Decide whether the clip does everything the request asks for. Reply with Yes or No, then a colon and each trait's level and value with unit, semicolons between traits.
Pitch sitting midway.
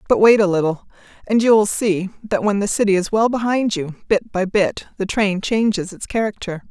No: high, 200 Hz